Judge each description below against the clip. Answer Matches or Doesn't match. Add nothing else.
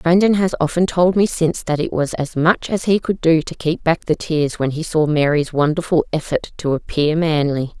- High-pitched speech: Doesn't match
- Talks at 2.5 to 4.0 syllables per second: Doesn't match